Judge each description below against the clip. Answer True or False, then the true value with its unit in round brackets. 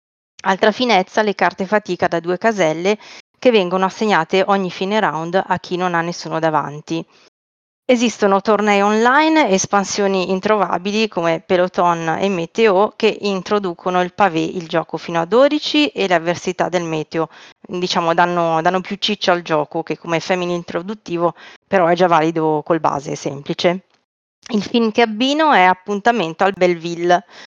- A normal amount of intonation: True (3.4 semitones)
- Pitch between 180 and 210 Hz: True (185 Hz)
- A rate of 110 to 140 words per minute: False (150 wpm)